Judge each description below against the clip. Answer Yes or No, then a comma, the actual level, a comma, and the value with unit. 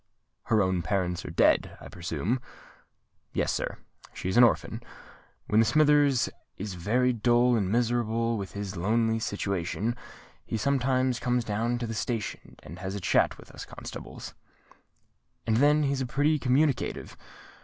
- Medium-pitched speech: No, low, 115 Hz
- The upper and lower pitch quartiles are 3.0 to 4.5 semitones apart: Yes, average, 3.9 semitones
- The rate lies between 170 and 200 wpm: No, average, 145 wpm